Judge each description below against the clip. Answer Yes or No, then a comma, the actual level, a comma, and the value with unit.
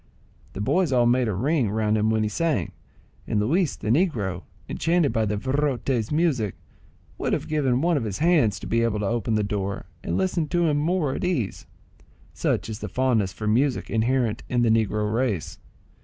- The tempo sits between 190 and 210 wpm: Yes, average, 200 wpm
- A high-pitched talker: No, low, 120 Hz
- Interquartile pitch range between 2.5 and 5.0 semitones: No, wide, 5.6 semitones